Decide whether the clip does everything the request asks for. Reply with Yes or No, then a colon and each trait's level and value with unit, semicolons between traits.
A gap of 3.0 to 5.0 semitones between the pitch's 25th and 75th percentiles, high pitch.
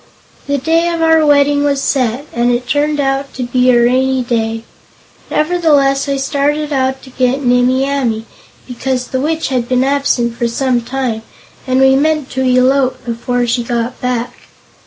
No: narrow, 2.4 semitones; very high, 260 Hz